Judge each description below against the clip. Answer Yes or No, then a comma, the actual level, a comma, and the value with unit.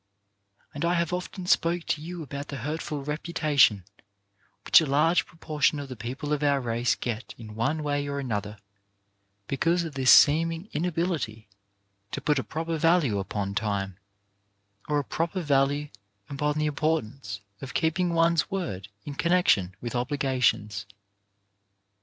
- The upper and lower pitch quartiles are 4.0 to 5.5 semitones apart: Yes, average, 5.2 semitones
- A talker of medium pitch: Yes, medium, 145 Hz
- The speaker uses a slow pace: No, average, 145 wpm